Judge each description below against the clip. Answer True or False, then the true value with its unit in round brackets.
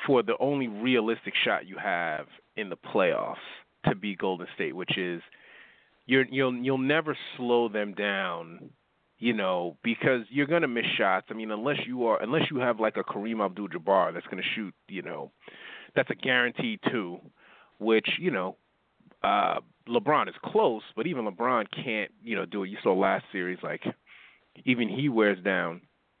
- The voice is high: False (120 Hz)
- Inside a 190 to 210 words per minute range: False (175 wpm)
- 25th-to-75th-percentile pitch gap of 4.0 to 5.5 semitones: True (4.5 semitones)